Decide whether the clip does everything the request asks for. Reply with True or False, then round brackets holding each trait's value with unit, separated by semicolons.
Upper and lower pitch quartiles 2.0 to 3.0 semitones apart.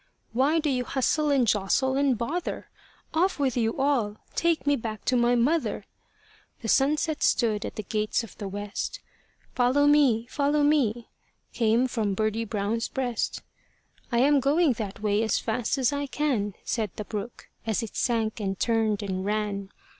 False (4.7 semitones)